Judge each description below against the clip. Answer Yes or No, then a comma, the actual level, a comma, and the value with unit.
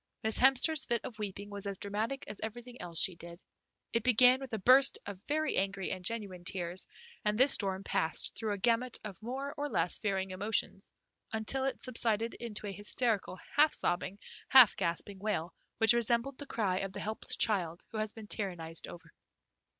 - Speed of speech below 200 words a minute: Yes, average, 185 wpm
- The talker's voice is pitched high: Yes, high, 210 Hz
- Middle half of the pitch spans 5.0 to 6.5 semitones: No, average, 4.1 semitones